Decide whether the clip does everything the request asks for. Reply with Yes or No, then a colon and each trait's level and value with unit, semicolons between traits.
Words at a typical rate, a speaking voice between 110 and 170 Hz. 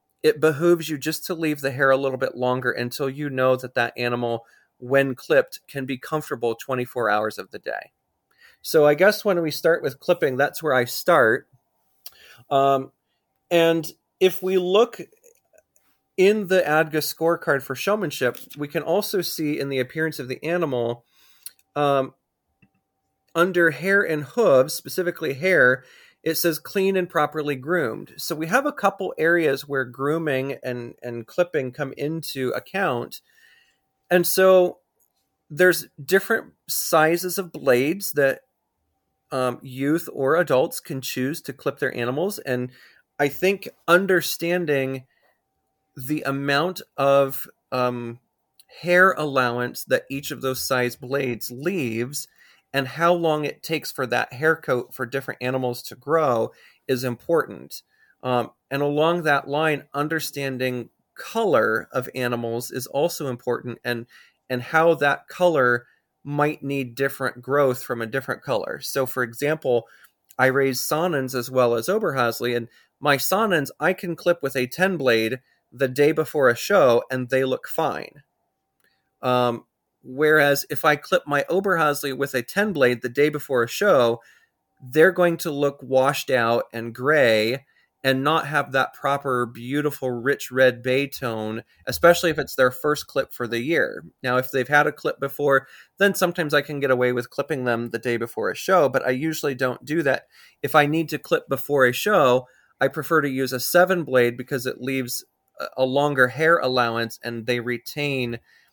Yes: average, 160 wpm; medium, 140 Hz